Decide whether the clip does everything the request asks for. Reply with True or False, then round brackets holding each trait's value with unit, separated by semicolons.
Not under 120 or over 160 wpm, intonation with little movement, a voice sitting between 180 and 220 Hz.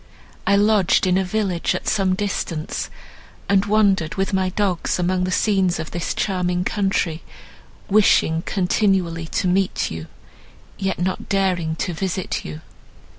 True (140 wpm; 2.2 semitones; 185 Hz)